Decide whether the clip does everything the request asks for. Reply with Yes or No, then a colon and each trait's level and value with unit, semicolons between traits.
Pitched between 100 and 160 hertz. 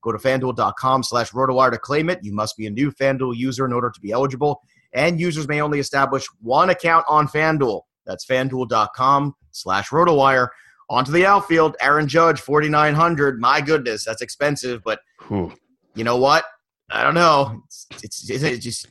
Yes: medium, 140 Hz